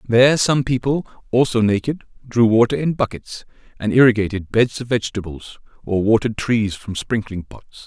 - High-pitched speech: No, low, 115 Hz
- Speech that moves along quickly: No, average, 155 wpm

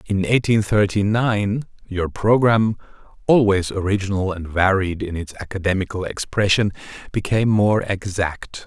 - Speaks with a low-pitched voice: Yes, low, 100 Hz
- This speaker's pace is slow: Yes, slow, 120 wpm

